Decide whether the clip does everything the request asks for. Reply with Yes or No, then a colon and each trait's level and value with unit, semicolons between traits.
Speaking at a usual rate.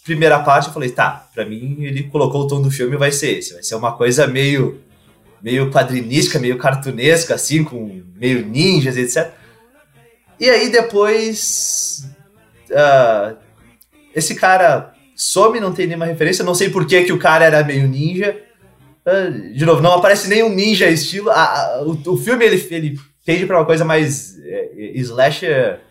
Yes: average, 170 wpm